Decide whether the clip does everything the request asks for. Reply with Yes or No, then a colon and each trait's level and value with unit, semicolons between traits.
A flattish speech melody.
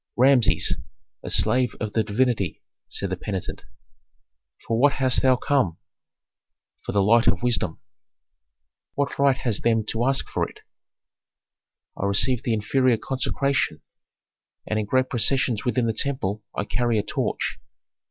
No: average, 3.7 semitones